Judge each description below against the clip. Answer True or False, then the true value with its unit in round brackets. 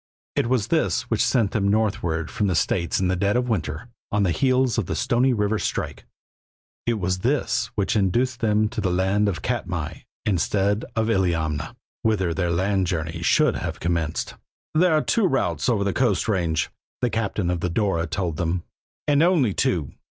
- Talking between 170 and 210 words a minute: True (180 wpm)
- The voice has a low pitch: True (100 Hz)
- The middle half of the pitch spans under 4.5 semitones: False (5.2 semitones)